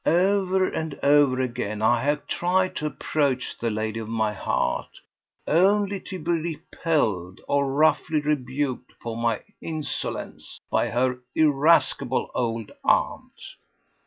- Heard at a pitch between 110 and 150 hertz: Yes, medium, 140 Hz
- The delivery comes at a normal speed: No, slow, 125 wpm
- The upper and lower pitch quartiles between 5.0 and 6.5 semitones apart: Yes, wide, 5.4 semitones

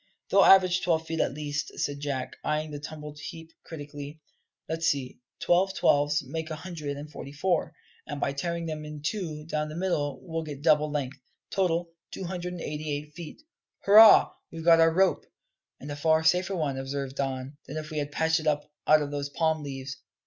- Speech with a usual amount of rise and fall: No, narrow, 2.3 semitones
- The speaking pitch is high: No, medium, 155 Hz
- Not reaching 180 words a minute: No, average, 200 wpm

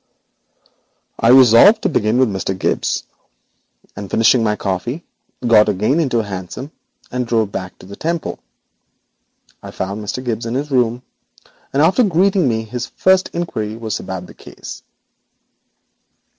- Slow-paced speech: No, average, 150 wpm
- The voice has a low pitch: Yes, low, 115 Hz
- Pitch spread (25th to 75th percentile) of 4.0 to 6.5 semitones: Yes, average, 4.6 semitones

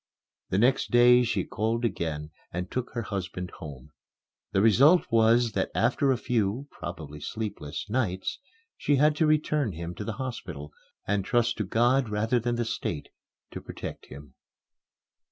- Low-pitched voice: Yes, low, 110 Hz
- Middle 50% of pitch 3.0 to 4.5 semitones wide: No, average, 5.3 semitones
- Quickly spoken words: No, average, 155 wpm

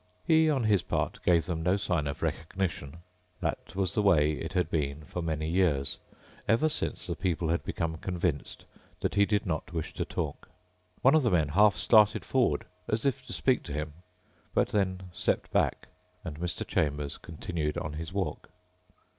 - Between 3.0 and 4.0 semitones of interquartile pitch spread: No, average, 4.5 semitones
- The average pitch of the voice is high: No, very low, 85 Hz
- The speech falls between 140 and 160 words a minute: No, average, 180 wpm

